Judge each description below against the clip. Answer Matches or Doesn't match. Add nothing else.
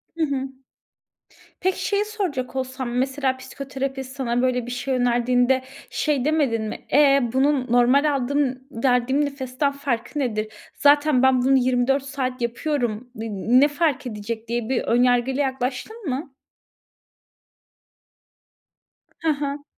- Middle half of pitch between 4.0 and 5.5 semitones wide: Doesn't match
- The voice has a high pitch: Matches